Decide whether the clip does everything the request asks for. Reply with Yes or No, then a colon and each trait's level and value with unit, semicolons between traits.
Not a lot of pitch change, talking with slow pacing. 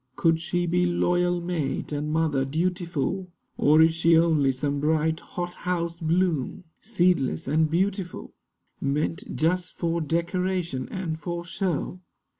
Yes: narrow, 2.3 semitones; slow, 125 wpm